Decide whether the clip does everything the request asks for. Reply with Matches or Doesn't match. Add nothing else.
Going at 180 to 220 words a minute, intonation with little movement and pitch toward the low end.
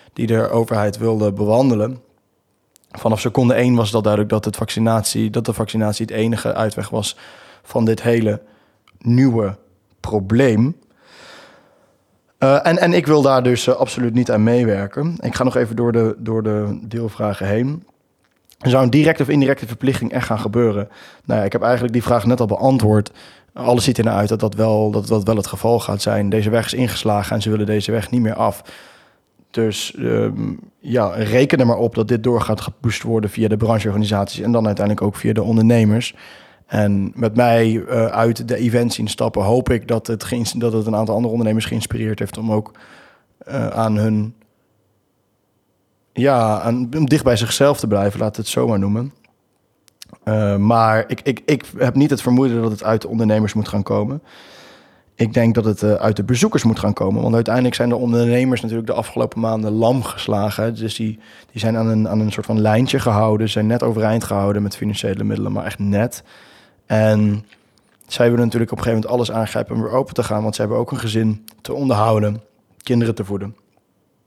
Matches